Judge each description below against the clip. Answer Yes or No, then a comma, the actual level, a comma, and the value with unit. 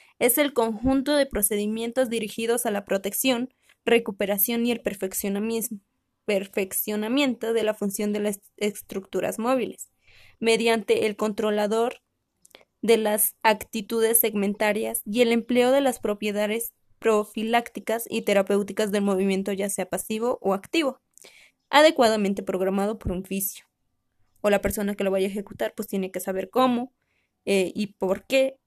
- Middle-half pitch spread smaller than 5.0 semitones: Yes, average, 2.7 semitones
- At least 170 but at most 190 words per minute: No, average, 135 wpm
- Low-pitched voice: No, high, 215 Hz